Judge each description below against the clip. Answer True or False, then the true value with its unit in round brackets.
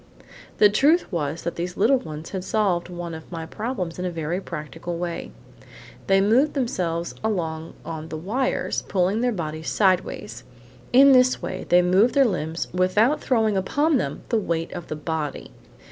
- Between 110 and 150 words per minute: False (170 wpm)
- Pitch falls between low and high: True (180 Hz)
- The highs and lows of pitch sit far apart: False (5.0 semitones)